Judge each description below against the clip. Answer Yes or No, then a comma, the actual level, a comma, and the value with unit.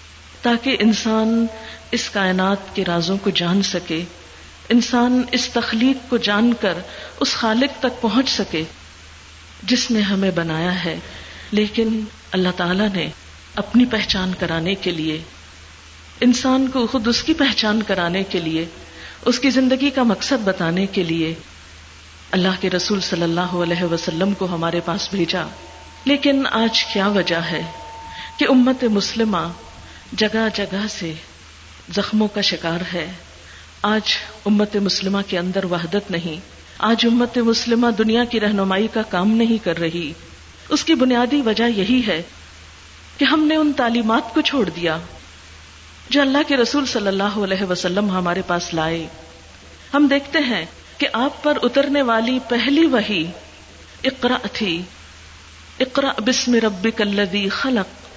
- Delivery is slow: No, average, 140 wpm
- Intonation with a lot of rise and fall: Yes, wide, 6.0 semitones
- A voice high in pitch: Yes, high, 200 Hz